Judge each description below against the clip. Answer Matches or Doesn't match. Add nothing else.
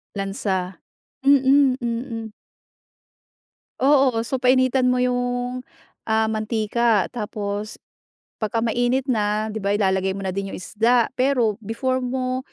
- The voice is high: Matches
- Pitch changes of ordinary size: Matches